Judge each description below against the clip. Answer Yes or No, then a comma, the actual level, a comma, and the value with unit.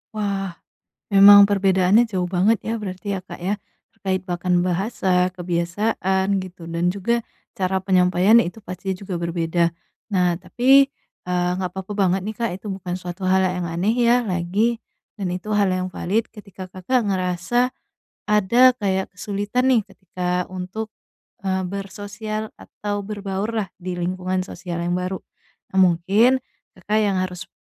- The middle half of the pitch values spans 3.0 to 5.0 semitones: No, narrow, 2.4 semitones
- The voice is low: No, high, 190 Hz